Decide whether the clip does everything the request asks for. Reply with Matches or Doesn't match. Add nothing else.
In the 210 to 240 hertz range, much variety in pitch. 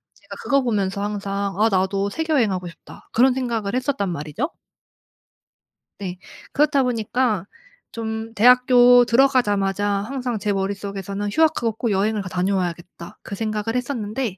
Doesn't match